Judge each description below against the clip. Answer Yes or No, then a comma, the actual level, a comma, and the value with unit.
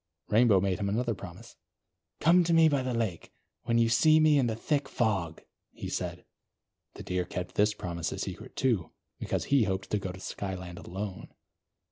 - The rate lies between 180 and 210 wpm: Yes, average, 185 wpm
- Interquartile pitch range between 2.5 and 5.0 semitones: No, wide, 5.4 semitones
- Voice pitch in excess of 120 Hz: No, low, 105 Hz